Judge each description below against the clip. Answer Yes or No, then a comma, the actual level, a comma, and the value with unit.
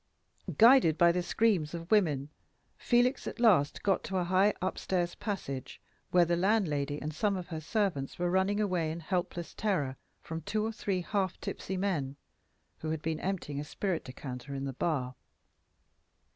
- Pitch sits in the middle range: Yes, medium, 175 Hz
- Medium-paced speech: Yes, average, 170 wpm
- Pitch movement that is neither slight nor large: Yes, average, 4.8 semitones